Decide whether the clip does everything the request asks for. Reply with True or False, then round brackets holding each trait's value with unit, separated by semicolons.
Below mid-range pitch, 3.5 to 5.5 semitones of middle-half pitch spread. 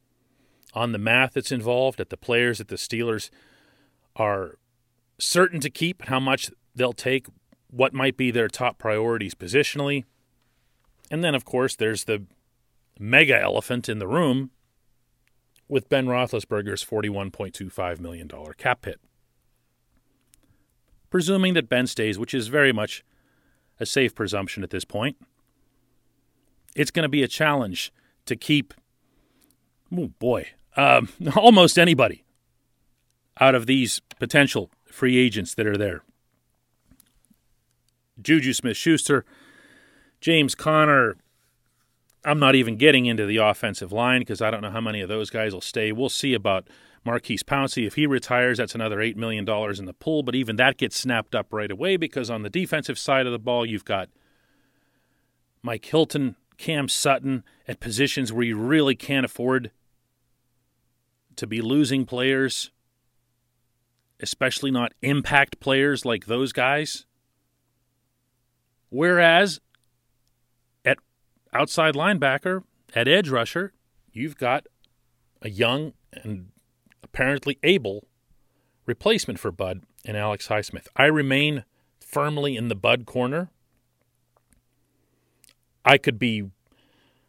False (125 Hz; 3.1 semitones)